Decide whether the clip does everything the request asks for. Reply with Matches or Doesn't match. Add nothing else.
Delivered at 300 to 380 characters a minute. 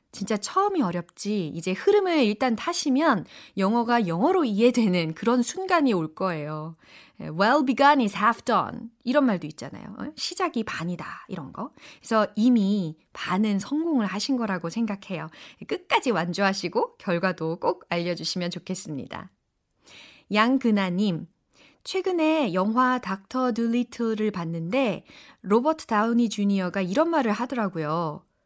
Matches